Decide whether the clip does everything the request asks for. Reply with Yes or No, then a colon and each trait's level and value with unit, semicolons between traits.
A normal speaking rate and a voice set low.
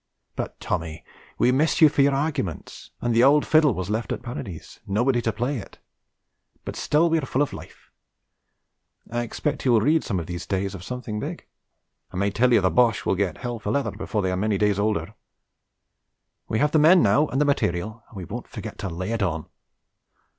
No: fast, 210 wpm; low, 115 Hz